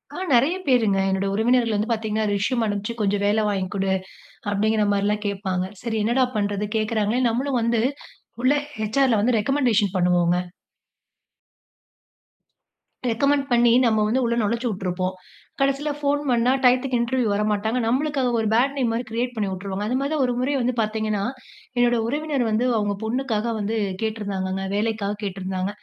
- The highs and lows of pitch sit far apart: No, average, 3.4 semitones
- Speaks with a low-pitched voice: No, high, 220 Hz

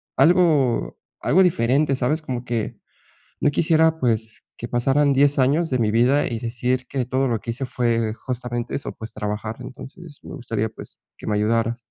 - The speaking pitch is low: Yes, low, 125 Hz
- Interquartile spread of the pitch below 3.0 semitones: No, average, 3.6 semitones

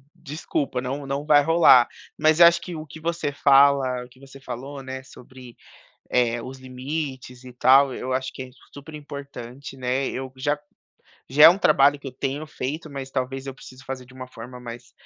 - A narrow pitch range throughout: Yes, narrow, 2.1 semitones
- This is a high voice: No, low, 135 Hz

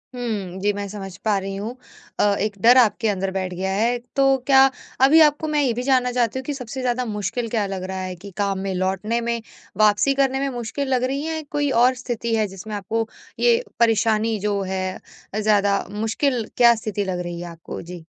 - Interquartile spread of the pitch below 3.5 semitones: No, average, 4.2 semitones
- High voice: Yes, high, 220 Hz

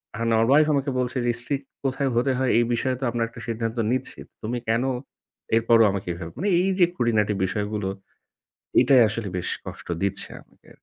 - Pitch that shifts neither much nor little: Yes, average, 3.2 semitones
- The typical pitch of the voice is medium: No, low, 120 Hz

